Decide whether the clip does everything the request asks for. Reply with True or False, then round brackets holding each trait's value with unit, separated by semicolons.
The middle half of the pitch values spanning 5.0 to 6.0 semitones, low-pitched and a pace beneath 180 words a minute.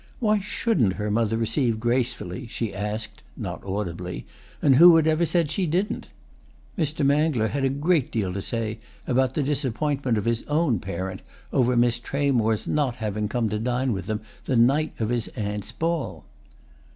True (5.4 semitones; 120 Hz; 170 wpm)